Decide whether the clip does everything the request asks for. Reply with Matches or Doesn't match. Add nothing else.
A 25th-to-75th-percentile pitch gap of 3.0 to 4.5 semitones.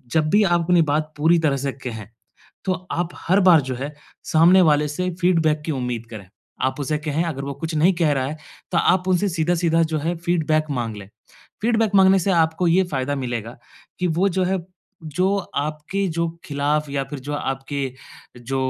Matches